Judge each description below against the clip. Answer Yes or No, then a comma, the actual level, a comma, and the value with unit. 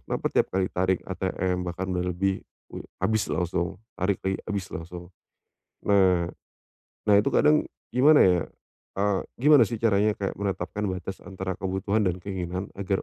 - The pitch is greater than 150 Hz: No, very low, 95 Hz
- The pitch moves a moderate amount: No, narrow, 2.0 semitones